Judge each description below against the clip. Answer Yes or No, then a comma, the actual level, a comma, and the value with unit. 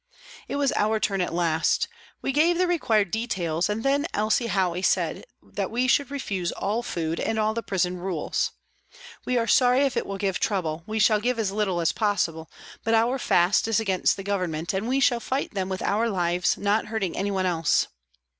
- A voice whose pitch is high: Yes, high, 205 Hz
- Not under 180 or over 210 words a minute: Yes, average, 200 wpm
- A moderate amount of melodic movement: Yes, average, 4.4 semitones